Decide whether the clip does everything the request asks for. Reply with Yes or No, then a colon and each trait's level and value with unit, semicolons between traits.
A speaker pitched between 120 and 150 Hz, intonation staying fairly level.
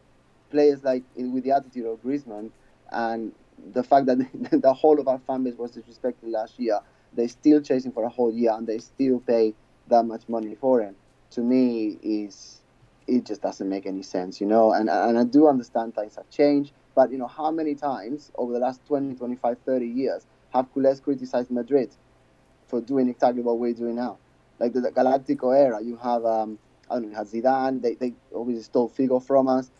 Yes: low, 125 Hz; narrow, 2.3 semitones